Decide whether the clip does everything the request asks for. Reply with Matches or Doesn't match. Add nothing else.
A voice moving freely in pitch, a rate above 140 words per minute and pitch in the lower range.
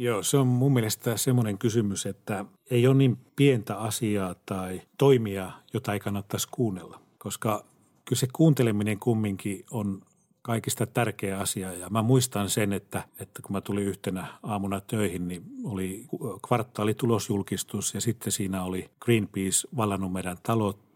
Doesn't match